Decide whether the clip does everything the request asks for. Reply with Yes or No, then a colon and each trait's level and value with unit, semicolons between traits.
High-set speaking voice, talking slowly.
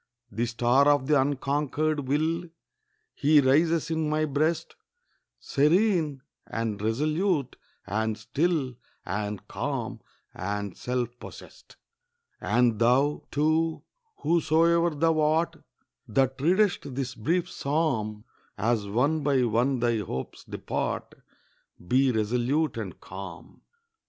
No: medium, 140 Hz; slow, 105 wpm